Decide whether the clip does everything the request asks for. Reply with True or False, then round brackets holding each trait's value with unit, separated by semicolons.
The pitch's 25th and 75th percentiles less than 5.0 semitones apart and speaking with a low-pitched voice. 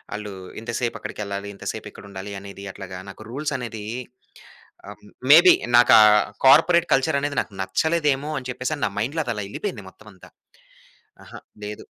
False (6.1 semitones; 120 Hz)